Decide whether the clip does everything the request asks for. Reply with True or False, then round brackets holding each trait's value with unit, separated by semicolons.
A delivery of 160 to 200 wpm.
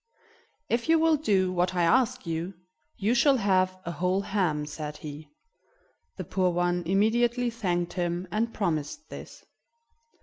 False (145 wpm)